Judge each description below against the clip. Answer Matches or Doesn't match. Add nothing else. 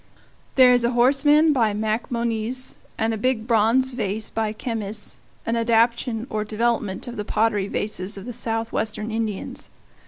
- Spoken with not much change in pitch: Matches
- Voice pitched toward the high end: Matches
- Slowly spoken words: Doesn't match